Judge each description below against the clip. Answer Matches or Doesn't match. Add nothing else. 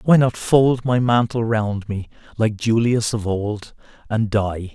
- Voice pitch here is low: Matches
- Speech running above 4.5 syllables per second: Doesn't match